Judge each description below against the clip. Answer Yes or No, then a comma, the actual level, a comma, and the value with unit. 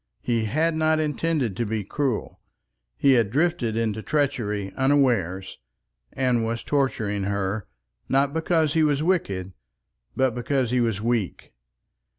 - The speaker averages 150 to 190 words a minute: No, slow, 135 wpm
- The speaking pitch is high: No, low, 125 Hz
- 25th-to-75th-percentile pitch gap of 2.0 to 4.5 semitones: No, average, 5.2 semitones